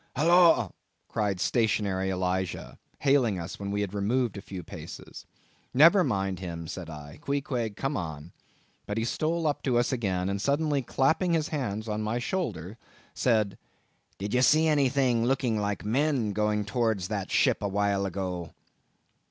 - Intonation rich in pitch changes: Yes, wide, 5.7 semitones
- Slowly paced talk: No, average, 155 wpm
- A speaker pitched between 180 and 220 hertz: No, low, 110 Hz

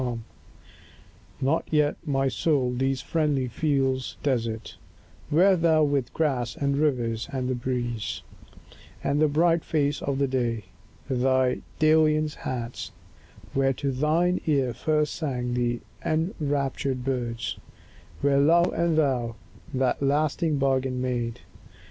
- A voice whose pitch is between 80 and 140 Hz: Yes, low, 135 Hz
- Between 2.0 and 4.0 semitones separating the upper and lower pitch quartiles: Yes, average, 3.4 semitones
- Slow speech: Yes, slow, 120 wpm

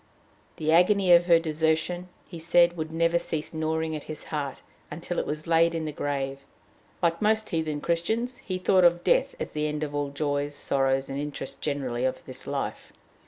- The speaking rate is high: No, average, 195 wpm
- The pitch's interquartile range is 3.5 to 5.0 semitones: No, average, 2.8 semitones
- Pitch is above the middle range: No, medium, 160 Hz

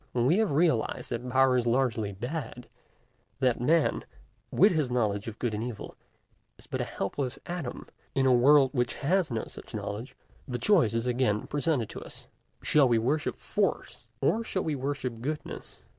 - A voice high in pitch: No, low, 130 Hz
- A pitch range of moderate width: Yes, average, 4.1 semitones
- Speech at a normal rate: Yes, average, 175 wpm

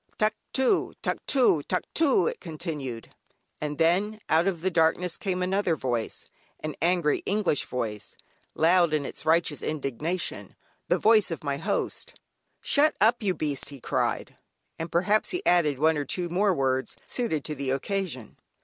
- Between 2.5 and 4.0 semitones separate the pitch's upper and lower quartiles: No, average, 4.7 semitones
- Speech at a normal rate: Yes, average, 150 wpm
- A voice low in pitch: No, medium, 165 Hz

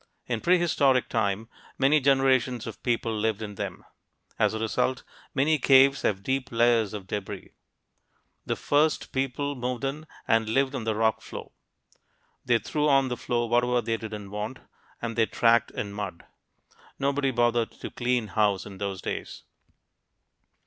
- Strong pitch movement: No, average, 3.4 semitones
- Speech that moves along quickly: No, average, 155 wpm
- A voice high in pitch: No, low, 120 Hz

